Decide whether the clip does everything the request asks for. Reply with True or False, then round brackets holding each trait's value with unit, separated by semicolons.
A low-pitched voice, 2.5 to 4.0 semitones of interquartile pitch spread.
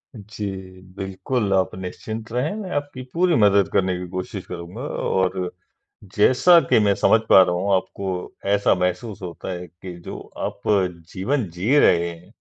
True (95 Hz; 3.7 semitones)